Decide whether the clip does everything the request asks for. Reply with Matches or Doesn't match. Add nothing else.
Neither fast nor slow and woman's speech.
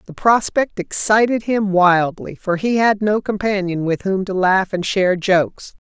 Matches